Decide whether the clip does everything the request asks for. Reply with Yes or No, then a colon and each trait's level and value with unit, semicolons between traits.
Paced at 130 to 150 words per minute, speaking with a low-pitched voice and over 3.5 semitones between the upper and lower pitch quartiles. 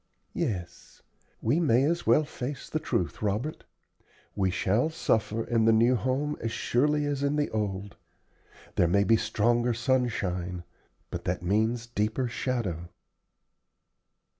Yes: slow, 135 wpm; low, 115 Hz; average, 4.5 semitones